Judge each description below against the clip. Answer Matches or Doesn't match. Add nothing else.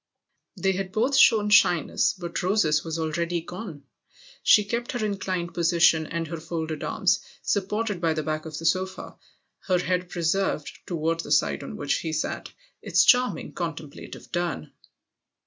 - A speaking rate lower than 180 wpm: Matches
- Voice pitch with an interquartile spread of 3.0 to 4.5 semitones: Matches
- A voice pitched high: Doesn't match